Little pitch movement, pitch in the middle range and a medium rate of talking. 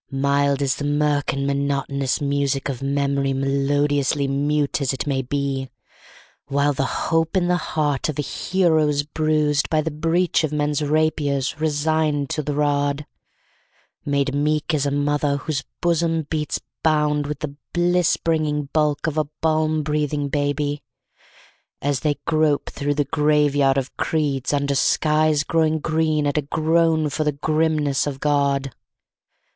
Yes: narrow, 1.7 semitones; medium, 145 Hz; average, 150 wpm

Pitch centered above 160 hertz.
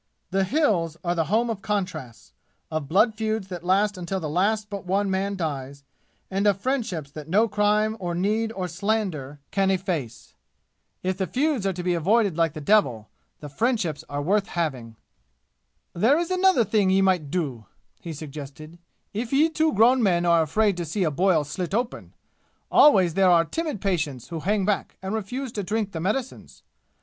Yes: high, 190 Hz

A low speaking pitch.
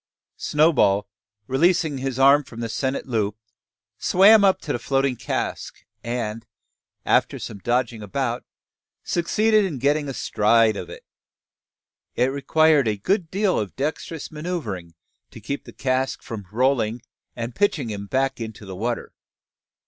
Yes: low, 130 Hz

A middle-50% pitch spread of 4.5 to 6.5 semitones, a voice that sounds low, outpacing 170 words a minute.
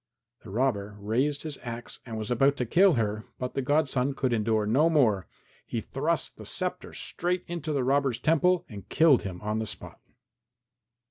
Yes: average, 5.3 semitones; low, 125 Hz; average, 180 wpm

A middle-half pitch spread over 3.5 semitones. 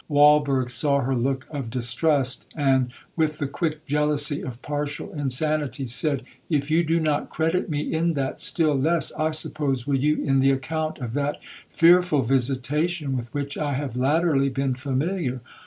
No: average, 2.7 semitones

